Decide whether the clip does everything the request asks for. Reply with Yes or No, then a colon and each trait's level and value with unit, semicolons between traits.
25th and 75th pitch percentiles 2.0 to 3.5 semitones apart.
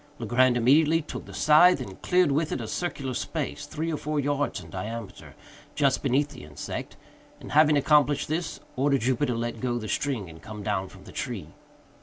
No: average, 4.4 semitones